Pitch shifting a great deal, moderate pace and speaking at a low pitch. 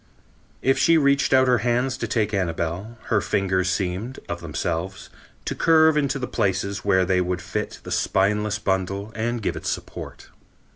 No: average, 5.0 semitones; average, 165 wpm; low, 100 Hz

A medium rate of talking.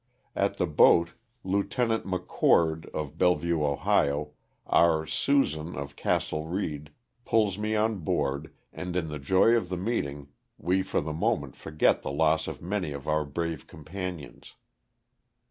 Yes: average, 150 wpm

